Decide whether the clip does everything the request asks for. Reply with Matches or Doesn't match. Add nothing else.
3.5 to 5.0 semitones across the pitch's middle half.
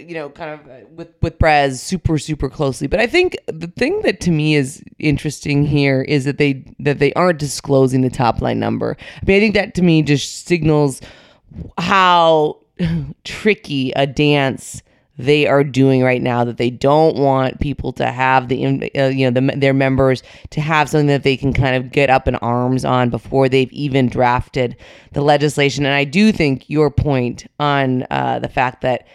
Doesn't match